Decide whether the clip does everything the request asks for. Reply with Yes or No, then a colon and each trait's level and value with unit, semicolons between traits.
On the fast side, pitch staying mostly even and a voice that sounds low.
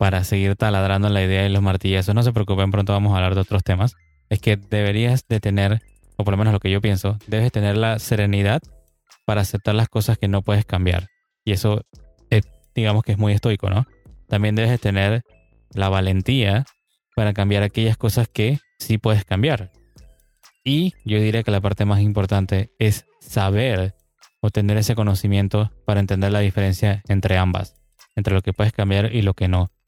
Yes: fast, 195 wpm; narrow, 1.9 semitones; low, 105 Hz